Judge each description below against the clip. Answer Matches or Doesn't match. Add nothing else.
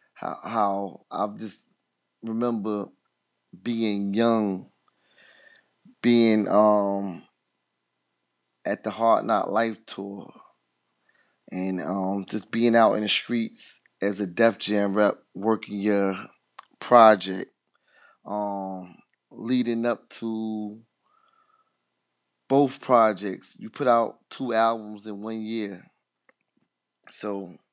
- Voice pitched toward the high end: Doesn't match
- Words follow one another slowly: Matches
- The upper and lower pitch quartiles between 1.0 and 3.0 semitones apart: Matches